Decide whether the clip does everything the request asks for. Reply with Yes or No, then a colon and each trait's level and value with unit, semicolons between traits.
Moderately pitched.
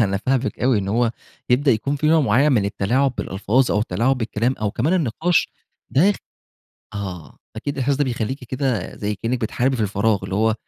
No: low, 120 Hz